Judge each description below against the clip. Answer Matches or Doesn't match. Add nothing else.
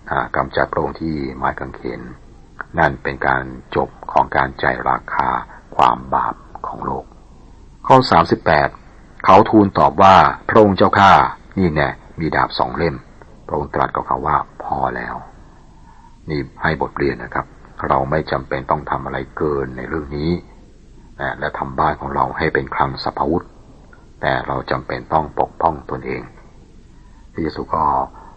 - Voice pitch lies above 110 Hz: Doesn't match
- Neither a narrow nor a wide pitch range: Matches